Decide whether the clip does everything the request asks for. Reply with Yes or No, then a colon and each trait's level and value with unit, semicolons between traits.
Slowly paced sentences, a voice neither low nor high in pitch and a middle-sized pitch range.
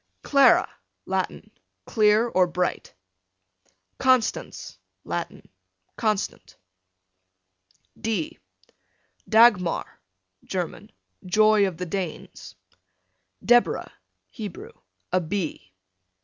No: slow, 70 wpm; high, 200 Hz; average, 3.6 semitones